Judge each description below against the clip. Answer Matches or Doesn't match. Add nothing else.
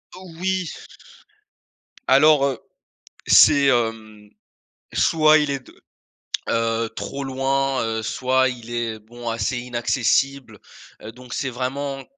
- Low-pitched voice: Matches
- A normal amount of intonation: Matches